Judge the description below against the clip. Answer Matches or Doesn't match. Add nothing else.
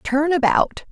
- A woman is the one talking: Matches